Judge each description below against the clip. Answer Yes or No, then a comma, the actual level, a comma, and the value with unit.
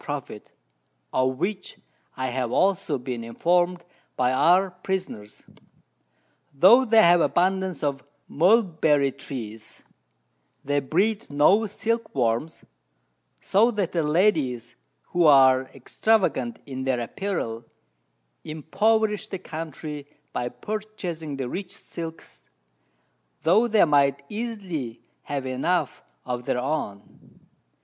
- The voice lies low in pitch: No, medium, 155 Hz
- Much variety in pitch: Yes, wide, 6.5 semitones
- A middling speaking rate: No, slow, 110 wpm